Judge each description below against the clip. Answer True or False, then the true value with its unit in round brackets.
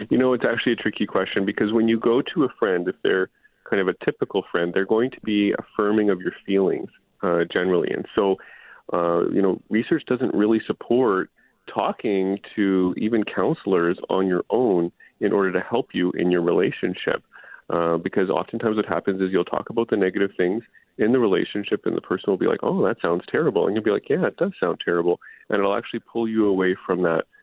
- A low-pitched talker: True (100 Hz)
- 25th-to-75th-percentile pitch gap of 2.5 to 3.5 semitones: True (3.2 semitones)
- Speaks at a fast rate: True (210 wpm)